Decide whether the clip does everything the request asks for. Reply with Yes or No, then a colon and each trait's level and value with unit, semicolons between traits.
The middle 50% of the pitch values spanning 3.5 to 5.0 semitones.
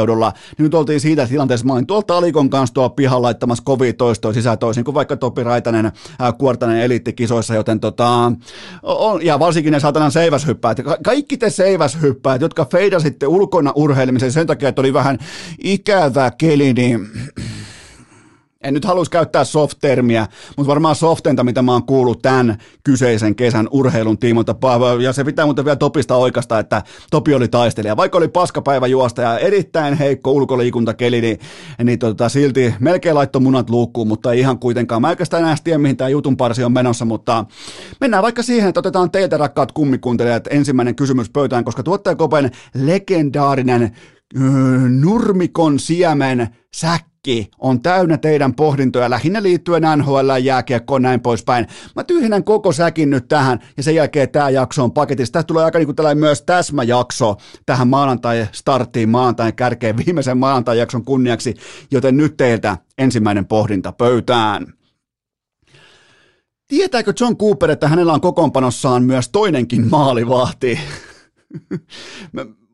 Yes: average, 4.2 semitones